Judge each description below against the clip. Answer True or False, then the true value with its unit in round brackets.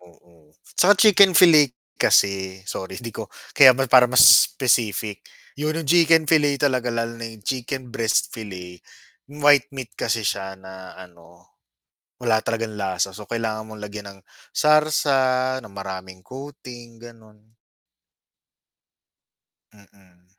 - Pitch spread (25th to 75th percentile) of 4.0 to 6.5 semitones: True (5.5 semitones)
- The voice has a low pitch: True (115 Hz)